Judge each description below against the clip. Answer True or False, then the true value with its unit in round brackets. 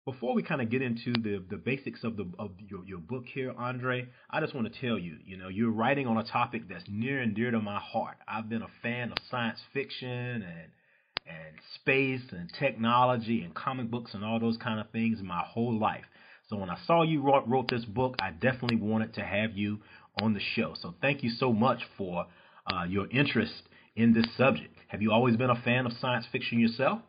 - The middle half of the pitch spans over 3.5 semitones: False (2.7 semitones)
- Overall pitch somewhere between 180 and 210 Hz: False (115 Hz)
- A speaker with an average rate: False (225 wpm)